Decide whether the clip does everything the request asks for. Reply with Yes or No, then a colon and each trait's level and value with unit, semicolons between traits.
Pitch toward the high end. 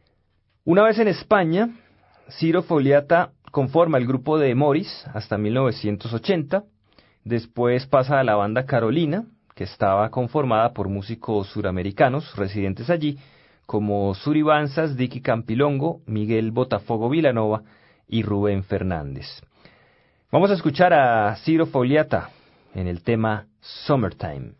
No: low, 125 Hz